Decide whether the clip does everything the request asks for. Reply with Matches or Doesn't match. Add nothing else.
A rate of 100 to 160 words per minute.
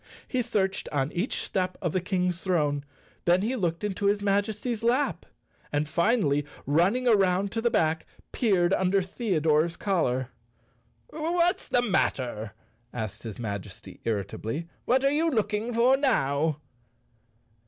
Matches